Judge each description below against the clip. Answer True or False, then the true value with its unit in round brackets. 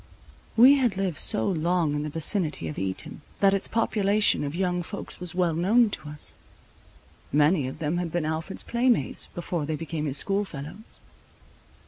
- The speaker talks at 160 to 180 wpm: True (170 wpm)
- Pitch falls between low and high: True (170 Hz)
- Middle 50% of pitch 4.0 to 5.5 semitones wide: True (4.8 semitones)